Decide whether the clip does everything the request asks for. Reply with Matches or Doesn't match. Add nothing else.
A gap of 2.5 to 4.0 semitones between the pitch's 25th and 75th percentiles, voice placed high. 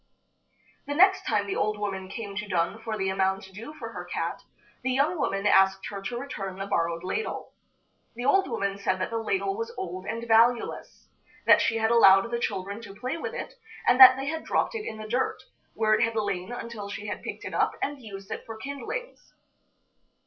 Doesn't match